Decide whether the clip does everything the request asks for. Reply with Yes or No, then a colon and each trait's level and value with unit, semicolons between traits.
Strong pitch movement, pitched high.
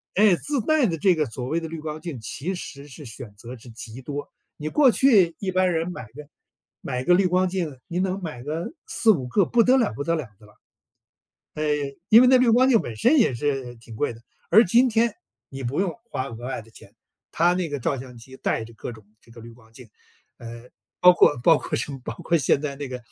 No: wide, 6.9 semitones; medium, 150 Hz